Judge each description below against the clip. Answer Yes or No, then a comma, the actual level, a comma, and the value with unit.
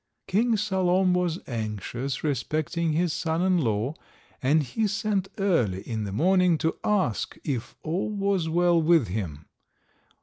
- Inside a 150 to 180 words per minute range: No, average, 140 wpm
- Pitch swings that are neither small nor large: No, wide, 7.2 semitones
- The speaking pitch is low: No, medium, 165 Hz